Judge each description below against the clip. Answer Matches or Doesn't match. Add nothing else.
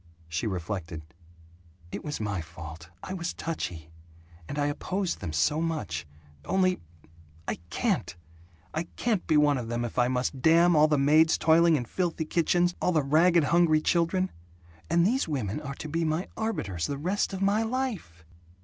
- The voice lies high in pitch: Doesn't match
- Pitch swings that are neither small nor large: Doesn't match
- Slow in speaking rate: Doesn't match